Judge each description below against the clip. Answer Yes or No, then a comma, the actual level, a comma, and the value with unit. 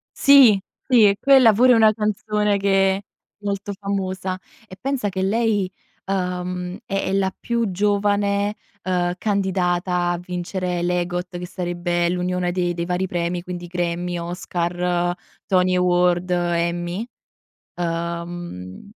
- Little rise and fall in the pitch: Yes, narrow, 2.3 semitones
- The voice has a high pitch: No, medium, 180 Hz